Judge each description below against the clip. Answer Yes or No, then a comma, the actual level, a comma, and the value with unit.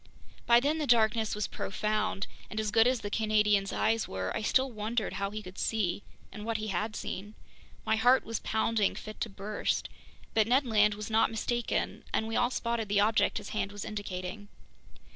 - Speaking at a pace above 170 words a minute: Yes, average, 190 wpm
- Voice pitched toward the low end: No, high, 215 Hz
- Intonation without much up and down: Yes, narrow, 1.7 semitones